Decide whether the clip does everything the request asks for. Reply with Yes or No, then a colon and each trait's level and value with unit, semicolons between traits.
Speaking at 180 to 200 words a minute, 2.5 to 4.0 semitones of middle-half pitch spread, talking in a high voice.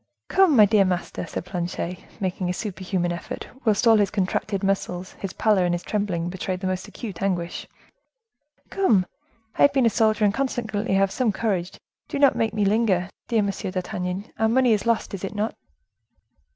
Yes: average, 190 wpm; average, 3.2 semitones; high, 200 Hz